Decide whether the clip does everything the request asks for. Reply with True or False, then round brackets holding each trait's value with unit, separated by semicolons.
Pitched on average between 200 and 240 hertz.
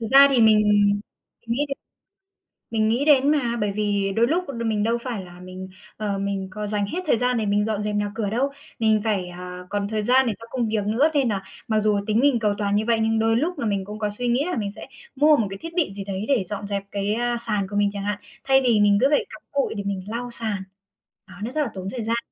True (215 Hz)